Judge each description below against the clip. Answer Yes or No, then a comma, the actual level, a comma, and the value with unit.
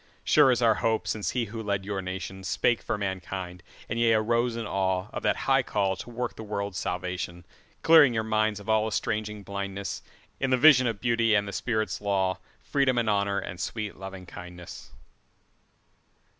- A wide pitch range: No, average, 3.3 semitones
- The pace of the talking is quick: No, average, 160 wpm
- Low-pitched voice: Yes, low, 105 Hz